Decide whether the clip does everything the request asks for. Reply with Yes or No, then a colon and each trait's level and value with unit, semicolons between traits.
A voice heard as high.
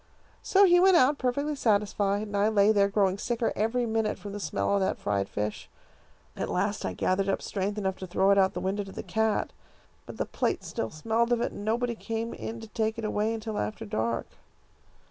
Yes: high, 210 Hz